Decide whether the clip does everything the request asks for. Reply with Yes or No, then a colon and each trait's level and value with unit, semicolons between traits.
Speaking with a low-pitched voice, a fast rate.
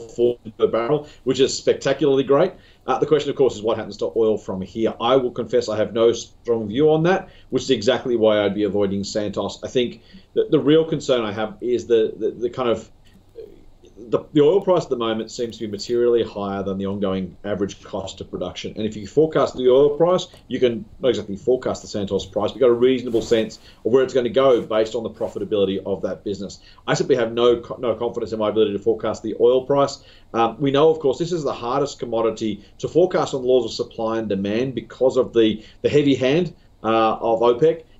Yes: low, 120 Hz; fast, 225 wpm